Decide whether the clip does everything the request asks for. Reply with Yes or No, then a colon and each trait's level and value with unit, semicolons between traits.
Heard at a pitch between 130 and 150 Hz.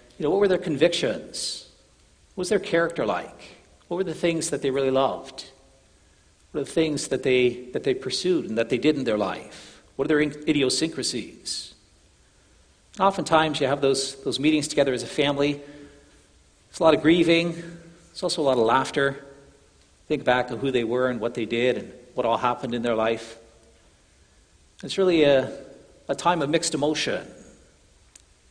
Yes: low, 135 Hz